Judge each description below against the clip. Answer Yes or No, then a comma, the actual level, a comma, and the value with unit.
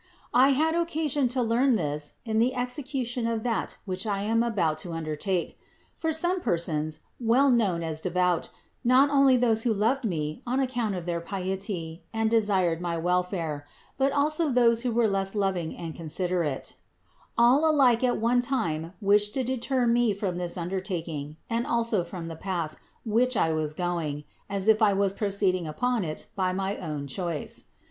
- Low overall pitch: No, high, 200 Hz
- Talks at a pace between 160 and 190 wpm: Yes, average, 175 wpm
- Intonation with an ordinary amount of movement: No, wide, 6.1 semitones